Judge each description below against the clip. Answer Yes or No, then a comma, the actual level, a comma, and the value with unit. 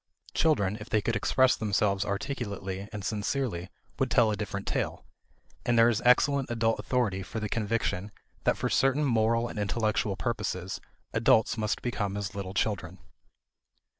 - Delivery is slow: No, average, 155 wpm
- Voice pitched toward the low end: Yes, low, 110 Hz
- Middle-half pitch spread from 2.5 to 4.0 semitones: Yes, average, 3.0 semitones